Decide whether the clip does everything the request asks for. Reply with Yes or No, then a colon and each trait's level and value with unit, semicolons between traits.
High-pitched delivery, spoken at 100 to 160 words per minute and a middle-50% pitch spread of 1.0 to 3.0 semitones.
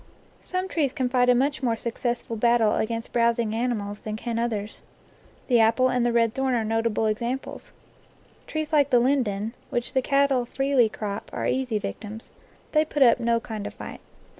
No: high, 235 Hz; average, 180 wpm; average, 2.7 semitones